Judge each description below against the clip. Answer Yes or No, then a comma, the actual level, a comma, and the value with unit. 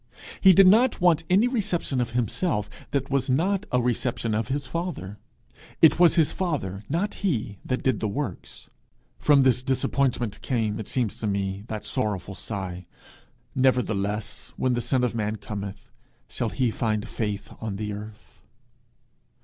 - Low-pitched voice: Yes, low, 120 Hz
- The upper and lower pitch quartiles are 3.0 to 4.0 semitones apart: No, wide, 5.6 semitones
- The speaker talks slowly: No, average, 155 wpm